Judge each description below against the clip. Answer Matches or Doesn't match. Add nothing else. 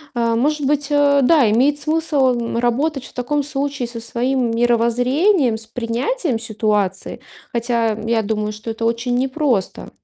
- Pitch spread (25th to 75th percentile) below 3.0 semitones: Doesn't match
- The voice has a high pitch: Matches